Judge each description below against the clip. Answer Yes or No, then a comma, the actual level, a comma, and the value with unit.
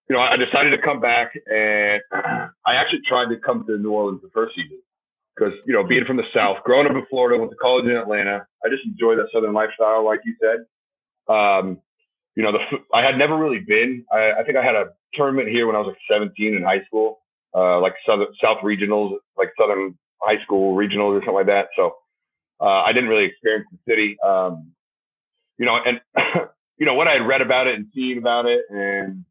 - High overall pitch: No, low, 115 Hz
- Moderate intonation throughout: No, wide, 7.1 semitones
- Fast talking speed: Yes, fast, 220 wpm